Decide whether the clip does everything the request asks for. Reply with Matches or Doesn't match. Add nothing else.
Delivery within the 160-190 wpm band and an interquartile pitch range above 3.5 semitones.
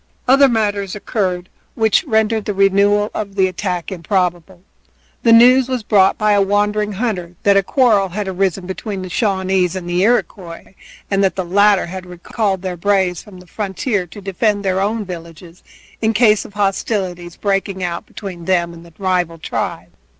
Doesn't match